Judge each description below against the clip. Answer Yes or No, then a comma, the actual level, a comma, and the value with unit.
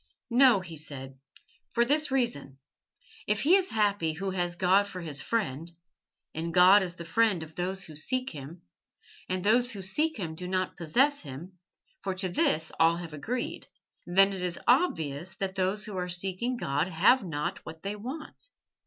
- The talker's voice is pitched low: No, medium, 185 Hz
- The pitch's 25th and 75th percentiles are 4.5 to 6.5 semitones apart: Yes, average, 4.8 semitones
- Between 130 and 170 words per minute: No, average, 180 wpm